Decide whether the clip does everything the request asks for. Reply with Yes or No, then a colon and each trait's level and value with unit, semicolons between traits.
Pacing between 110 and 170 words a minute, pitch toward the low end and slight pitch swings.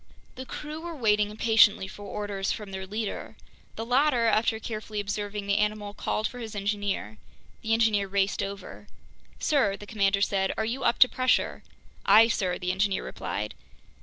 No: average, 165 wpm; high, 210 Hz; narrow, 2.3 semitones